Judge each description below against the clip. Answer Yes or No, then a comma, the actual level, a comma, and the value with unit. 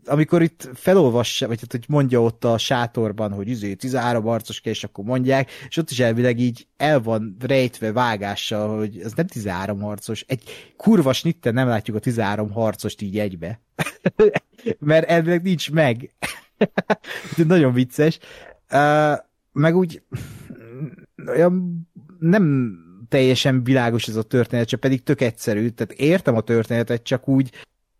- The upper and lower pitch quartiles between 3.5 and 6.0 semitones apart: Yes, average, 4.7 semitones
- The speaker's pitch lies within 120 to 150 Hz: Yes, low, 125 Hz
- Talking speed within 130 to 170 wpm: Yes, average, 140 wpm